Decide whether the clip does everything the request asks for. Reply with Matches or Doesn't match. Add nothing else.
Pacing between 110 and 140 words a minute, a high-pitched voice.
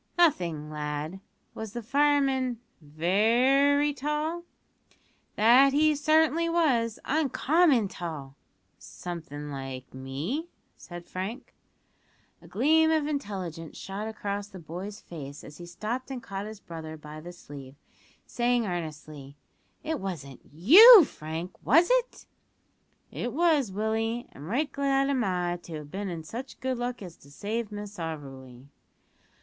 Matches